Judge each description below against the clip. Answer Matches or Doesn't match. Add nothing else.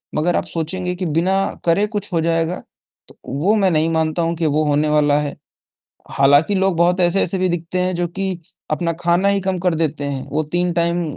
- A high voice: Doesn't match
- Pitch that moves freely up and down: Doesn't match